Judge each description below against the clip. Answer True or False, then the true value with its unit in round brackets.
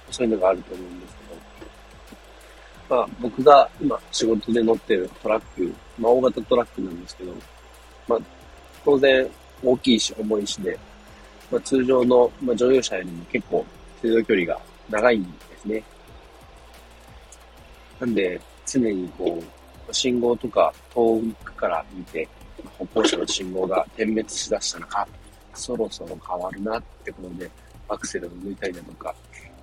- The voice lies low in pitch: True (95 Hz)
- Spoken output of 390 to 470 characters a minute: False (285 characters per minute)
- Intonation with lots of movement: True (7.7 semitones)